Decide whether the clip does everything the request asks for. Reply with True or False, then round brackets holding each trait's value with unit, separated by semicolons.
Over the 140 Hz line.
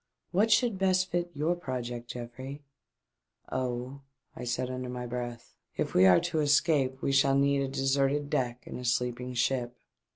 False (130 Hz)